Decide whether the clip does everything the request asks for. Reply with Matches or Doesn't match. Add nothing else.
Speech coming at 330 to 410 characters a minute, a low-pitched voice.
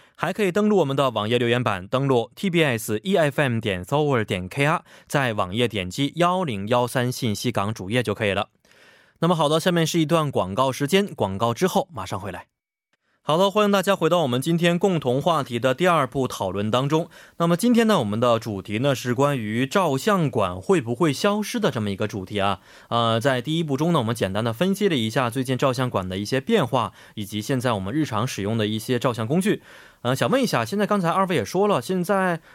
Matches